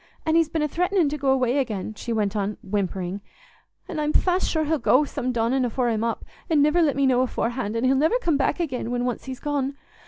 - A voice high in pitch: Yes, very high, 265 Hz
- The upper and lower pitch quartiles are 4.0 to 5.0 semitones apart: Yes, average, 4.6 semitones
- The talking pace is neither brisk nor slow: No, fast, 240 wpm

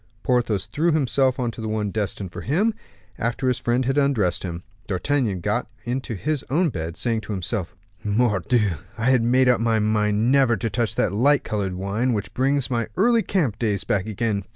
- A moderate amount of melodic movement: Yes, average, 4.1 semitones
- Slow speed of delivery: No, average, 190 wpm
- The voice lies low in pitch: Yes, low, 115 Hz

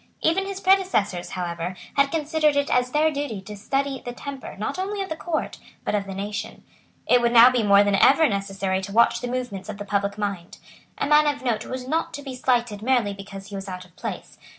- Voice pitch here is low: No, high, 235 Hz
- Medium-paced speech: No, fast, 225 wpm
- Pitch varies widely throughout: Yes, wide, 6.1 semitones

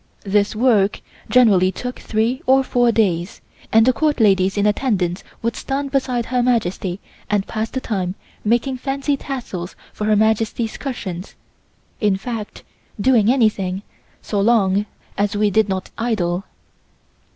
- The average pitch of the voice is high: Yes, high, 220 Hz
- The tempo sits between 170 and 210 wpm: No, average, 140 wpm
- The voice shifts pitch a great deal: No, average, 4.0 semitones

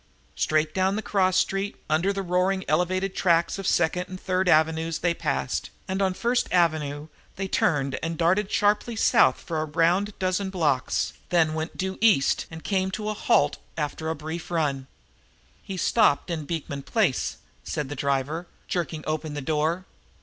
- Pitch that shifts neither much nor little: Yes, average, 3.5 semitones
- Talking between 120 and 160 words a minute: No, average, 170 wpm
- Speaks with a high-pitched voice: No, medium, 170 Hz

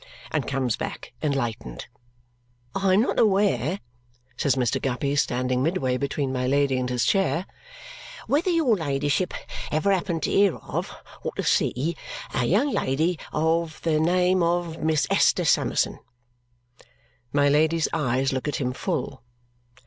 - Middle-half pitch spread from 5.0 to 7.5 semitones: Yes, average, 5.3 semitones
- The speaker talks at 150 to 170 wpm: No, average, 140 wpm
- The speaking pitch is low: No, medium, 150 Hz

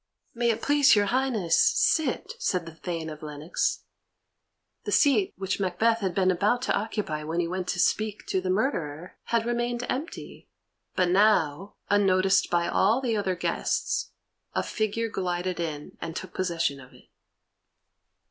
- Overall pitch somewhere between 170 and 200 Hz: Yes, high, 190 Hz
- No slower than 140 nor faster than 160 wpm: Yes, average, 155 wpm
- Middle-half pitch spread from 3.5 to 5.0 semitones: Yes, average, 4.6 semitones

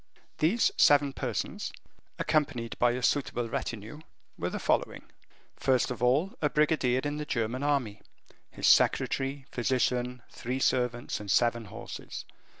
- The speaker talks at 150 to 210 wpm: No, slow, 135 wpm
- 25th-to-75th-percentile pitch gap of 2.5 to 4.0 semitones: Yes, average, 3.2 semitones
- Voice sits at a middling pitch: No, low, 125 Hz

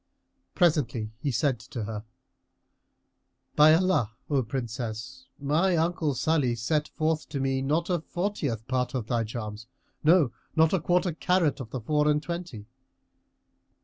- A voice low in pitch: No, medium, 145 Hz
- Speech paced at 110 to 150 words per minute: Yes, average, 145 wpm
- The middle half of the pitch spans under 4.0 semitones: No, average, 5.3 semitones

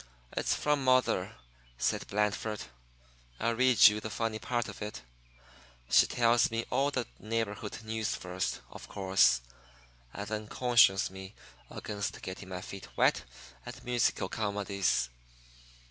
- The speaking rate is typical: No, slow, 130 wpm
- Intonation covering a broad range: No, average, 3.1 semitones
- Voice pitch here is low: Yes, low, 110 Hz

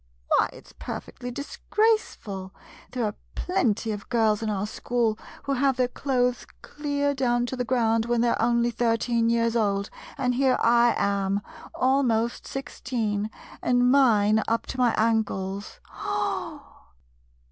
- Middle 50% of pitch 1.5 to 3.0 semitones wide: Yes, narrow, 2.6 semitones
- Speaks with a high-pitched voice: Yes, high, 235 Hz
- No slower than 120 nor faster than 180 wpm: Yes, average, 150 wpm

